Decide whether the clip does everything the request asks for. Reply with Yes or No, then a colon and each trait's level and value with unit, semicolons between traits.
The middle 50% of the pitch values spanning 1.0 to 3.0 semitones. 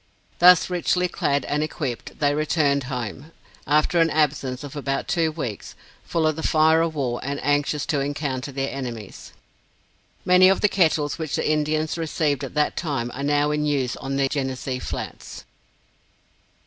Yes: narrow, 2.6 semitones